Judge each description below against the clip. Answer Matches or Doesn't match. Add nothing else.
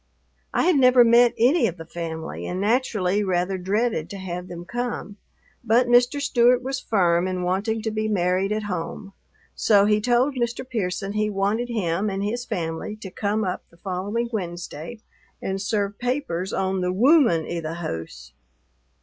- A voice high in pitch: Matches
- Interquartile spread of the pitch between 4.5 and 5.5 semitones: Matches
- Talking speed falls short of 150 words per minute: Doesn't match